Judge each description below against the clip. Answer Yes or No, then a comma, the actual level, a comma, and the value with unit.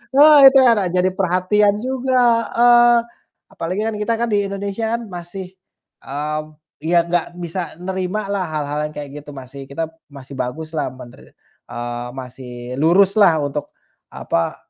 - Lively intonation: Yes, wide, 6.1 semitones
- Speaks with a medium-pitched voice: Yes, medium, 175 Hz